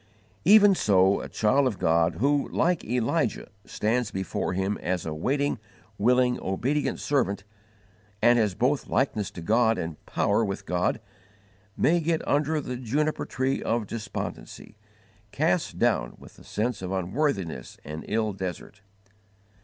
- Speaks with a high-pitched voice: No, low, 115 Hz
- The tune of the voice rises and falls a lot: Yes, wide, 6.3 semitones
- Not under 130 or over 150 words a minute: Yes, average, 140 wpm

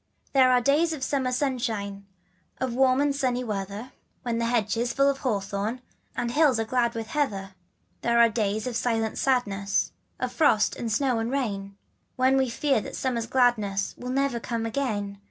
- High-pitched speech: Yes, high, 240 Hz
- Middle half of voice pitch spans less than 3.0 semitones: No, average, 3.5 semitones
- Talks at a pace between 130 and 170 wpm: No, average, 190 wpm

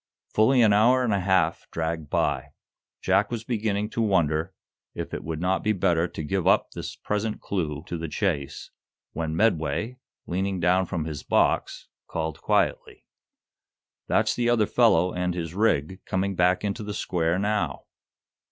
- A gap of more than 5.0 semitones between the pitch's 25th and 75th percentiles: No, average, 4.3 semitones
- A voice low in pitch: Yes, very low, 95 Hz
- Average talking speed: Yes, average, 160 wpm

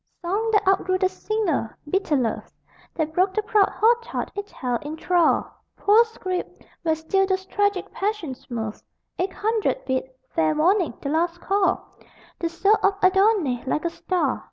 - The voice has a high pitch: Yes, very high, 370 Hz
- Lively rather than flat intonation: No, average, 4.4 semitones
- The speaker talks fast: No, average, 165 wpm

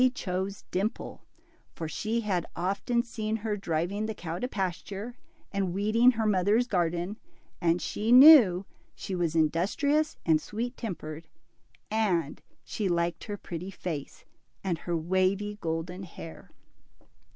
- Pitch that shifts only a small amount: No, average, 4.0 semitones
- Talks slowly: Yes, slow, 130 wpm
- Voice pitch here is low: No, high, 190 Hz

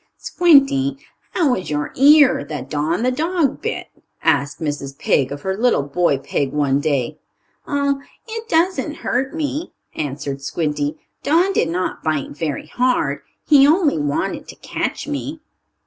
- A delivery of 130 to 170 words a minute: Yes, average, 150 wpm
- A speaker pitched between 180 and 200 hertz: Yes, high, 190 Hz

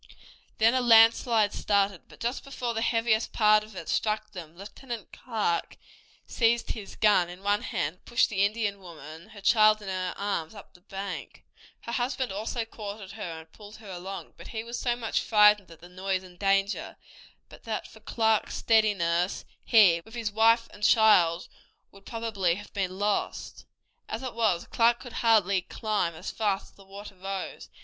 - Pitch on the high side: Yes, high, 205 Hz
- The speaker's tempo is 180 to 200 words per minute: Yes, average, 185 wpm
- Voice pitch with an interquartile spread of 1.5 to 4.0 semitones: Yes, average, 3.1 semitones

